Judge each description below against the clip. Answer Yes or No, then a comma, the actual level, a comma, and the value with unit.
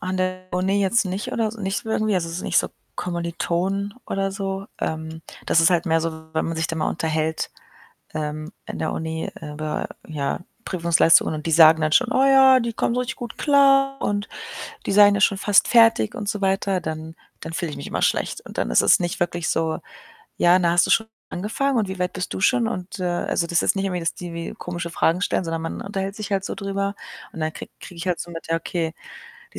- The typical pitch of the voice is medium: Yes, medium, 180 Hz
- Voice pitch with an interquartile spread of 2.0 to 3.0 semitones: No, average, 3.6 semitones